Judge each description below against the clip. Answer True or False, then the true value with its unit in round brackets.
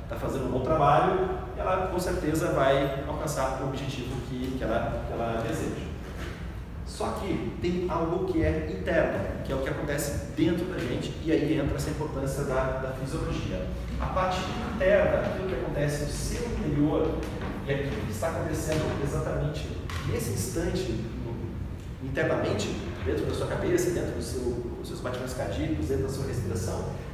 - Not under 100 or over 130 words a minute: False (165 wpm)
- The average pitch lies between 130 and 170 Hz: True (135 Hz)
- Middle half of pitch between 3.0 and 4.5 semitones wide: False (2.5 semitones)